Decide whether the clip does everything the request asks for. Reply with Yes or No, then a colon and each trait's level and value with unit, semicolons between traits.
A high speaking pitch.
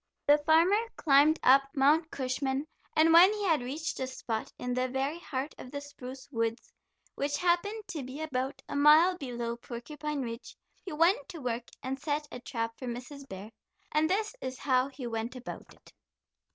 Yes: very high, 275 Hz